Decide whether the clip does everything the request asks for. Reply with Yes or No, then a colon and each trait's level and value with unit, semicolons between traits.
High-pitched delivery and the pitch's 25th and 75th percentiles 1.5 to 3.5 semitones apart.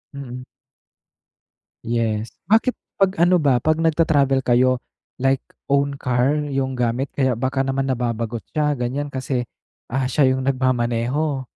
No: low, 130 Hz; narrow, 2.4 semitones